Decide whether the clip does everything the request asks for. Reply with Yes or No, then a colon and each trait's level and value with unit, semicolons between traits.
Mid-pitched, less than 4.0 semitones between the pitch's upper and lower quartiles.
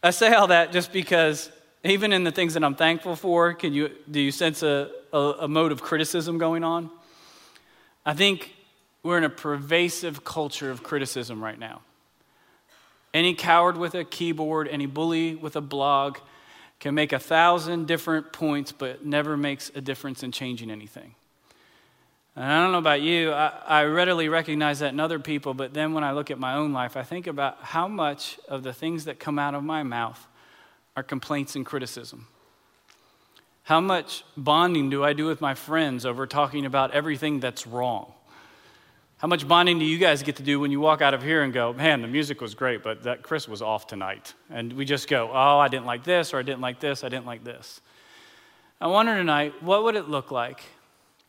Yes: medium, 150 Hz; average, 3.1 semitones